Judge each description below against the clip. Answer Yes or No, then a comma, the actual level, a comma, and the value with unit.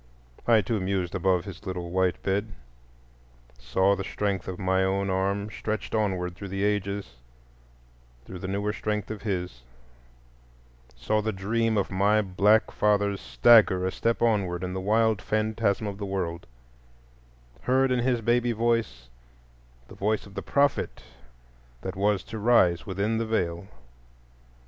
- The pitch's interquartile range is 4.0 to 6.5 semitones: No, narrow, 2.6 semitones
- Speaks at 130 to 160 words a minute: Yes, average, 150 wpm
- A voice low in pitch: Yes, low, 100 Hz